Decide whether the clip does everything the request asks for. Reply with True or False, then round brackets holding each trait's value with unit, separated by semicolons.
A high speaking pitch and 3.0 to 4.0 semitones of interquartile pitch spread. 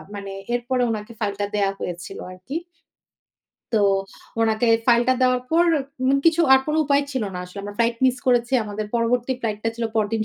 True (230 Hz; 3.5 semitones)